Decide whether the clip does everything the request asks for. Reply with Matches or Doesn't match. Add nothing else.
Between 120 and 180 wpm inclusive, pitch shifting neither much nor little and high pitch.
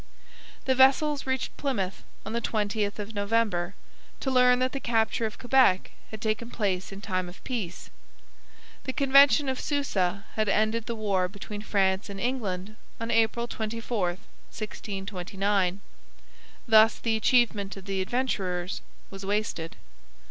Matches